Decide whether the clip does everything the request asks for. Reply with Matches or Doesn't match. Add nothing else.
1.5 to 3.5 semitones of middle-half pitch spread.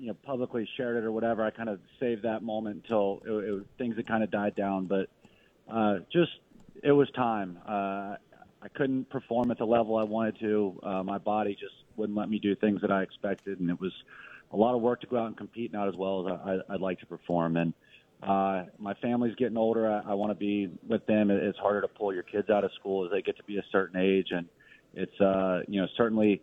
Matches